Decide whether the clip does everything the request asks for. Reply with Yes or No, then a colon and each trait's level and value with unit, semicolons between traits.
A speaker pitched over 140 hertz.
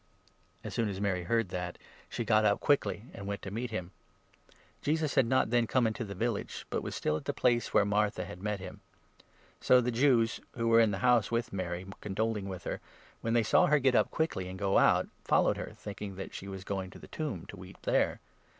No: low, 105 Hz